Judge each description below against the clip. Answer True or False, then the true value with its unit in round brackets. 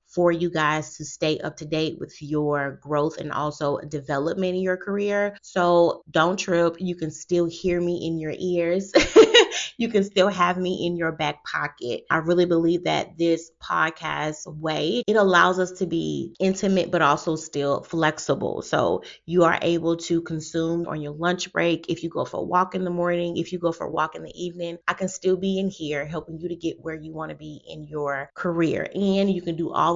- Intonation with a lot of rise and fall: False (2.4 semitones)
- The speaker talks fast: True (210 wpm)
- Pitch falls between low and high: True (170 Hz)